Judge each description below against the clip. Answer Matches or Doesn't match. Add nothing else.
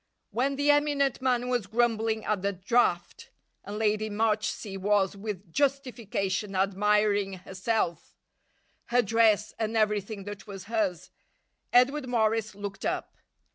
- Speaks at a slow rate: Matches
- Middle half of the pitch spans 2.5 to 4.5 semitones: Matches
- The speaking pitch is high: Matches